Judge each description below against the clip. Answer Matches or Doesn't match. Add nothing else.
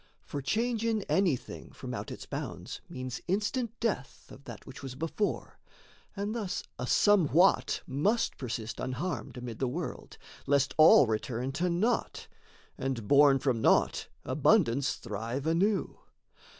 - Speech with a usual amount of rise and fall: Doesn't match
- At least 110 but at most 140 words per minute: Matches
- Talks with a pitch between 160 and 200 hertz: Doesn't match